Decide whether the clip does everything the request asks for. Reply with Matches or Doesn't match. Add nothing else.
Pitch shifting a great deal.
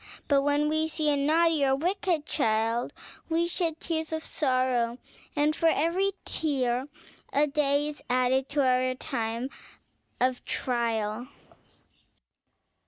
Doesn't match